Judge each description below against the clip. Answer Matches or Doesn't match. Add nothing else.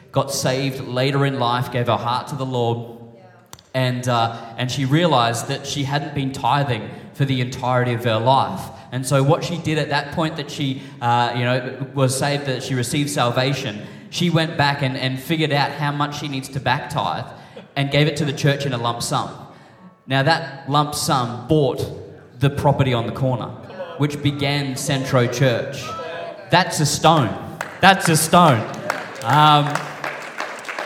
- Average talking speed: Matches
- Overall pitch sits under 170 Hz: Matches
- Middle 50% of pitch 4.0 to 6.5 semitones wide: Doesn't match